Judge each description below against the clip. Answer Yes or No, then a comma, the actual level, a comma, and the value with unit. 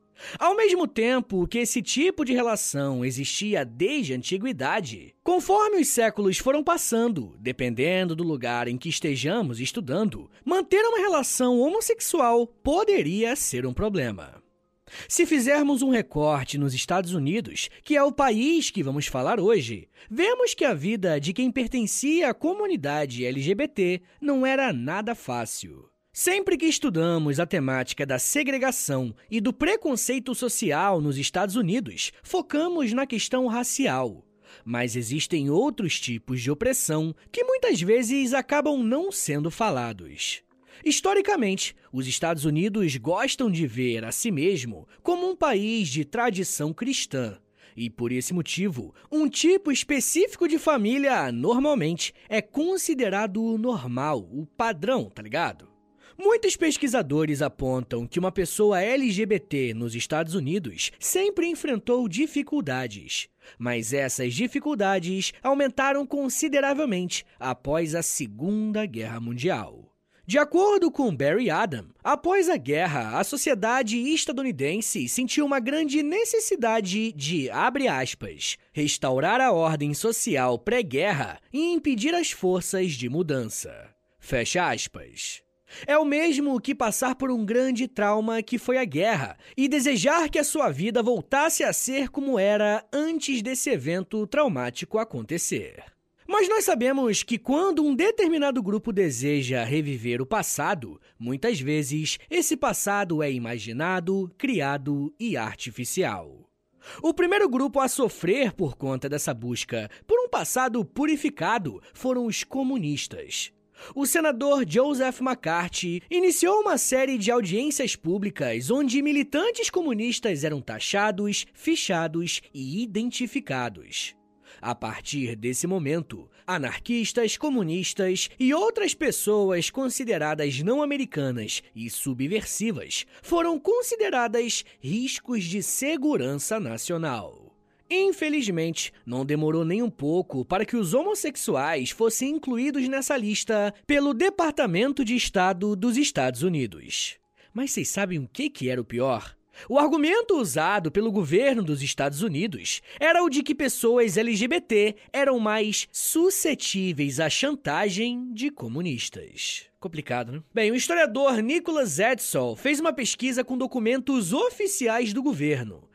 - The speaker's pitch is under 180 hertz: No, high, 230 Hz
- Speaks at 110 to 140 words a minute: Yes, average, 125 wpm